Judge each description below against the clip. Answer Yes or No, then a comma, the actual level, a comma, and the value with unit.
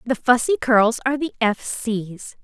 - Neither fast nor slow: Yes, average, 175 wpm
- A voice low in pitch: No, high, 235 Hz